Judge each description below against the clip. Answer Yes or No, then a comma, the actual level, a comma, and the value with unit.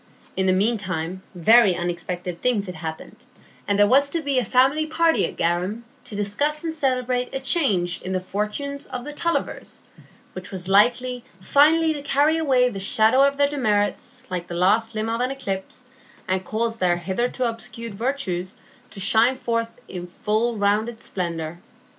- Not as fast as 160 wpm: No, average, 170 wpm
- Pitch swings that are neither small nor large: No, wide, 5.8 semitones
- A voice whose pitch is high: Yes, high, 225 Hz